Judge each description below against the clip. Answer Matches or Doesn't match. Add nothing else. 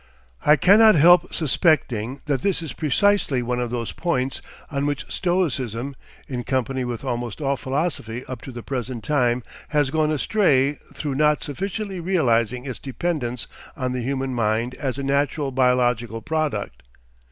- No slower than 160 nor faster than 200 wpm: Doesn't match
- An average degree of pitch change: Matches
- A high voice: Doesn't match